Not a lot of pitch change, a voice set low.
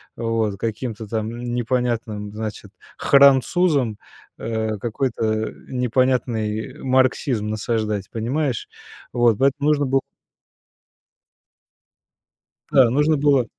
No: average, 3.2 semitones; low, 120 Hz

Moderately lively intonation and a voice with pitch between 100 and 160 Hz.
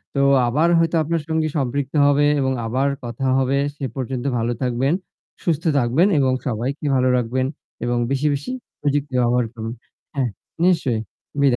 Yes: average, 3.0 semitones; low, 135 Hz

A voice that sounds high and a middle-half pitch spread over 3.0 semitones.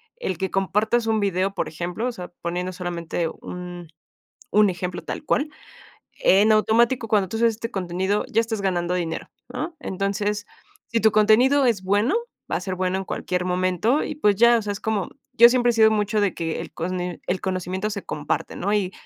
Yes: high, 200 Hz; average, 3.4 semitones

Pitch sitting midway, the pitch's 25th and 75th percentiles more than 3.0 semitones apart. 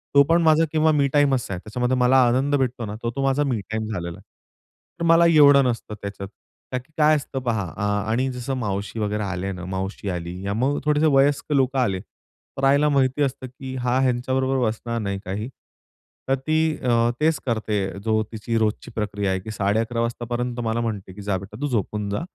No: low, 120 Hz; average, 4.6 semitones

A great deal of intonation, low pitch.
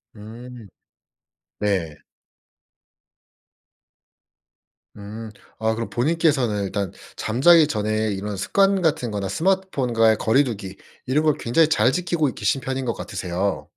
Yes: wide, 6.1 semitones; low, 115 Hz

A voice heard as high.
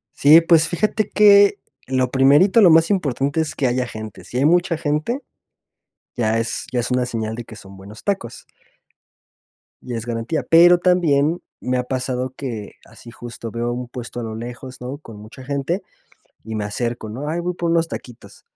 No: low, 130 Hz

